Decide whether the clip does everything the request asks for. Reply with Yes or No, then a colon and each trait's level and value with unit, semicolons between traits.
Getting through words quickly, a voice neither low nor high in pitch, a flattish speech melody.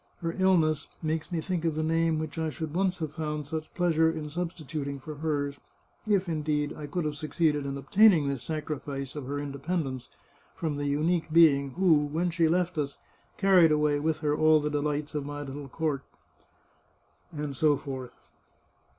No: average, 180 wpm; medium, 155 Hz; narrow, 2.2 semitones